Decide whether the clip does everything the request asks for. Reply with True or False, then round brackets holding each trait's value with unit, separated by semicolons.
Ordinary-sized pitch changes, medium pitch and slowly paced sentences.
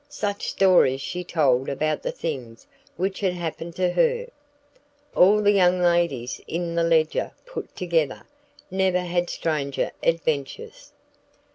True (3.2 semitones; 170 Hz; 130 wpm)